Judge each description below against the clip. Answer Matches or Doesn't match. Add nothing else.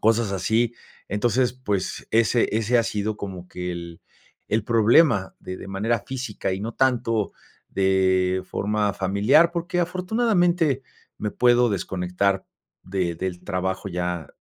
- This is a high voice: Doesn't match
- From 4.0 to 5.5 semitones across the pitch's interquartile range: Matches